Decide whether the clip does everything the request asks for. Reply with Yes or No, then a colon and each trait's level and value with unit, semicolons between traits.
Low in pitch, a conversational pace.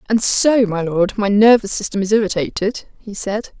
No: high, 210 Hz; average, 185 wpm